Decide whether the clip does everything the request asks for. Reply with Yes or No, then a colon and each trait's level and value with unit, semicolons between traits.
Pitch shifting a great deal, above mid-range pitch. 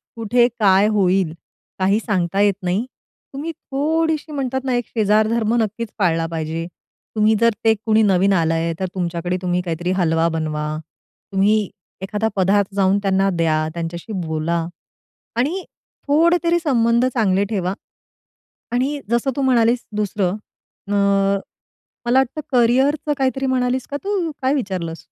Yes: wide, 5.9 semitones; high, 210 Hz